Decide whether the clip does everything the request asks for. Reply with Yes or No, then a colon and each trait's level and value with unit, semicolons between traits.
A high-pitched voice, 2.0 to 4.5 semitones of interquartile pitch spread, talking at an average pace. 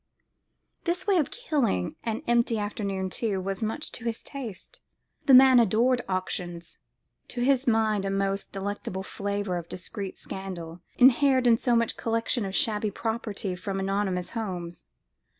Yes: high, 210 Hz; average, 3.8 semitones; average, 145 wpm